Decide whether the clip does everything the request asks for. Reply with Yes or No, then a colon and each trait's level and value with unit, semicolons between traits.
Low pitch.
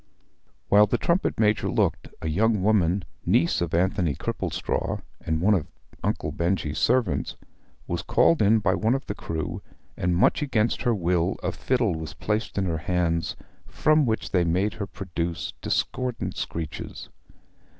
Yes: very low, 95 Hz